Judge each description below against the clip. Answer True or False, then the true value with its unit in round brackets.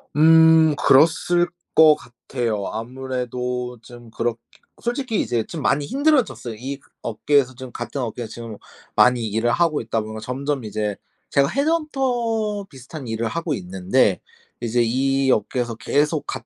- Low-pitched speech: True (130 Hz)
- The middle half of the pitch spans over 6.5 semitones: False (5.5 semitones)